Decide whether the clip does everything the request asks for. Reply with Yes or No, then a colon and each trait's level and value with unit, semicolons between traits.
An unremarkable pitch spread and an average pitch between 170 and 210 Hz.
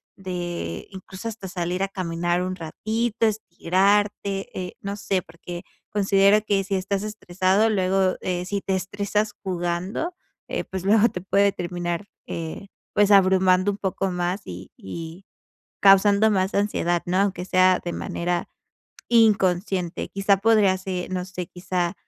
No: narrow, 2.1 semitones; high, 190 Hz